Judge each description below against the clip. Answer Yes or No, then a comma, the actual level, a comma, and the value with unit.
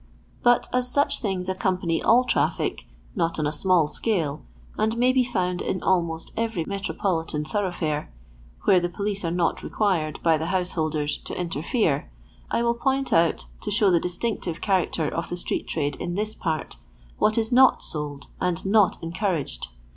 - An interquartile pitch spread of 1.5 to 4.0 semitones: No, average, 4.7 semitones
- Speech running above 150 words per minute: Yes, average, 170 wpm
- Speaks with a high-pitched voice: No, medium, 180 Hz